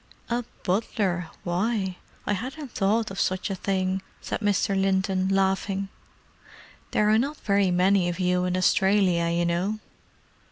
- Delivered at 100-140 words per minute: Yes, slow, 135 wpm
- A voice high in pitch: Yes, high, 195 Hz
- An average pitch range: No, narrow, 2.1 semitones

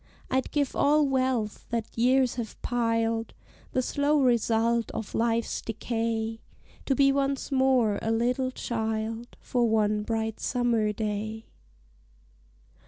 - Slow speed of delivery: Yes, slow, 120 wpm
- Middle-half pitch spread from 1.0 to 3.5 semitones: Yes, narrow, 2.5 semitones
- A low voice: No, high, 230 Hz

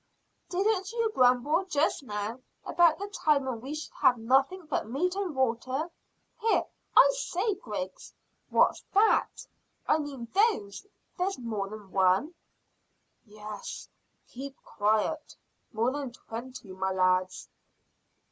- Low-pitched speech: No, very high, 265 Hz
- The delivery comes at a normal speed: No, slow, 125 wpm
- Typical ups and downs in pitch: No, wide, 8.6 semitones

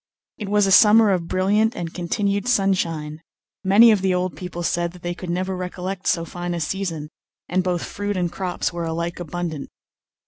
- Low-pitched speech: No, medium, 180 Hz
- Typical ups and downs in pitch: No, narrow, 2.2 semitones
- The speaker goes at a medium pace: Yes, average, 185 wpm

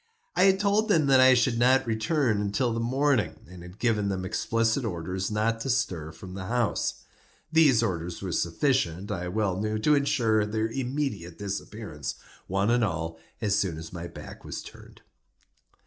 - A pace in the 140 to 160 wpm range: No, average, 175 wpm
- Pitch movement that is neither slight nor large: No, wide, 5.7 semitones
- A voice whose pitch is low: Yes, low, 110 Hz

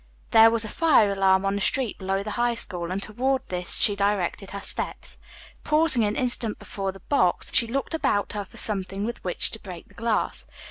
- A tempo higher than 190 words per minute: Yes, fast, 205 wpm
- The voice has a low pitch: No, high, 205 Hz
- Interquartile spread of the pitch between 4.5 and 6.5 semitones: No, average, 3.3 semitones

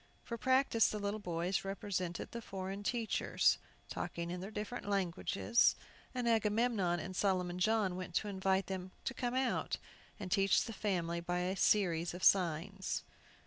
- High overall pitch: Yes, high, 195 Hz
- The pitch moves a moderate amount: Yes, average, 3.1 semitones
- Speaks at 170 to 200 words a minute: No, average, 155 wpm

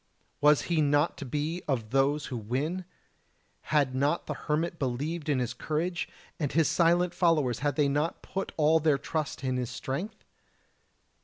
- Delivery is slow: No, average, 165 wpm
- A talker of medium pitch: Yes, medium, 150 Hz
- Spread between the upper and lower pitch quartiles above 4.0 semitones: No, average, 3.4 semitones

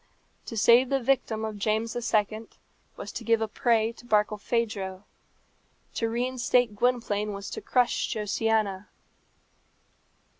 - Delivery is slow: Yes, slow, 120 wpm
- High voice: Yes, high, 225 Hz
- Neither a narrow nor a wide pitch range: No, narrow, 2.3 semitones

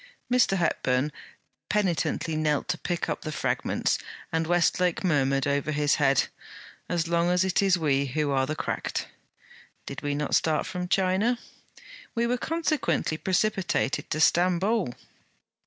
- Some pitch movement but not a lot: Yes, average, 4.0 semitones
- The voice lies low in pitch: No, medium, 170 Hz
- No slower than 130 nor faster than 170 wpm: Yes, average, 140 wpm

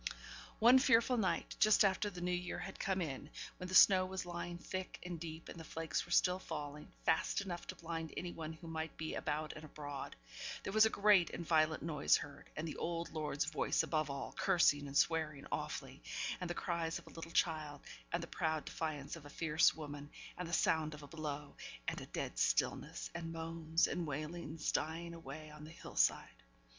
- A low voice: No, medium, 165 Hz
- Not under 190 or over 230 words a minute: Yes, fast, 205 wpm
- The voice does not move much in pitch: Yes, narrow, 2.3 semitones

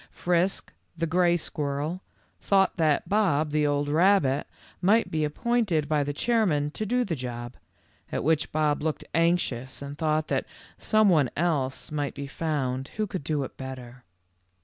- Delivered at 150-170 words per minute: Yes, average, 160 wpm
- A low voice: No, medium, 155 Hz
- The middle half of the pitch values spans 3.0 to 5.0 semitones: Yes, average, 3.9 semitones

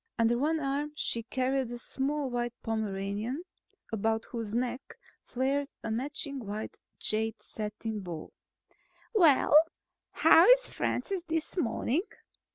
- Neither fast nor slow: No, slow, 120 wpm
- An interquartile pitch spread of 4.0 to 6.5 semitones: Yes, average, 4.3 semitones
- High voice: Yes, high, 245 Hz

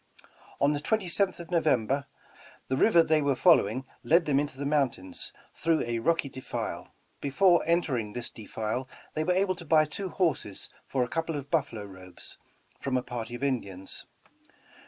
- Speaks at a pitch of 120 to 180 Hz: Yes, medium, 140 Hz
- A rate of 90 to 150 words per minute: No, average, 165 wpm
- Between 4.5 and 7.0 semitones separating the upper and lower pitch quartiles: Yes, average, 5.1 semitones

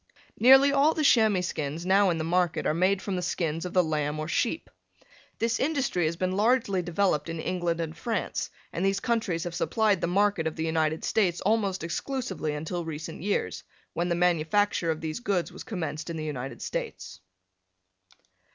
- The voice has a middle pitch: Yes, medium, 175 Hz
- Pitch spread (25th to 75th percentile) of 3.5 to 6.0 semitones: Yes, average, 4.2 semitones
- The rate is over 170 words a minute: Yes, average, 185 wpm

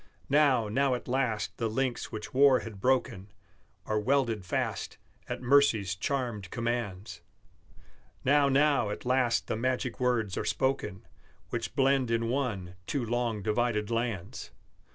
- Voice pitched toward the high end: No, low, 120 Hz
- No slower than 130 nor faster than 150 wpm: Yes, slow, 135 wpm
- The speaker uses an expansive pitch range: No, average, 3.8 semitones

